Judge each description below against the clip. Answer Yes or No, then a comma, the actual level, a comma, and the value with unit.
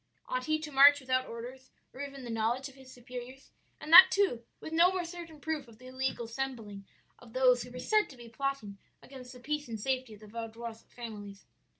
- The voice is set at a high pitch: Yes, very high, 255 Hz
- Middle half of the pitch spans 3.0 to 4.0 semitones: Yes, average, 3.5 semitones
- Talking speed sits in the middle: No, fast, 215 wpm